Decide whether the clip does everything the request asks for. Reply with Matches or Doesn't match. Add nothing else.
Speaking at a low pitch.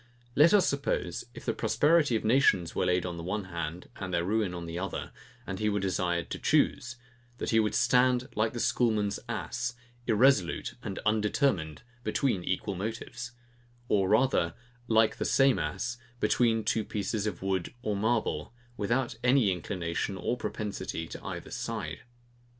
Matches